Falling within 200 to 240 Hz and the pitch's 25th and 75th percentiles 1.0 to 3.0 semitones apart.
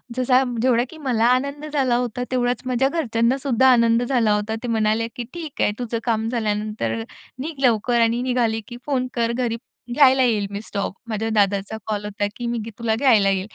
Yes: high, 235 Hz; narrow, 2.6 semitones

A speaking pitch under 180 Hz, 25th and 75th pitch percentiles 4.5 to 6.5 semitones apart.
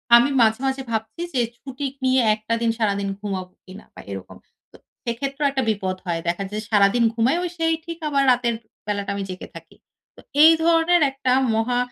No: high, 235 Hz; average, 5.2 semitones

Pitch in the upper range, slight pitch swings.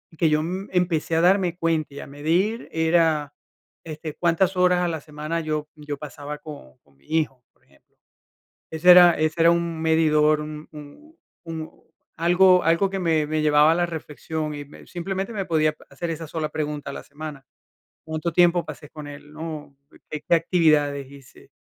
No: medium, 160 Hz; narrow, 2.2 semitones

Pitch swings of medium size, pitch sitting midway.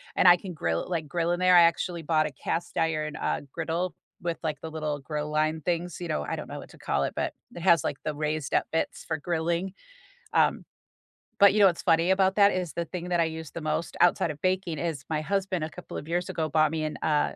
No: narrow, 2.3 semitones; medium, 165 Hz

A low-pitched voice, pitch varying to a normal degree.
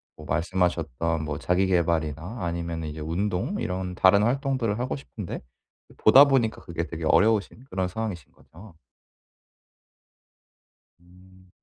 Yes: very low, 90 Hz; average, 4.4 semitones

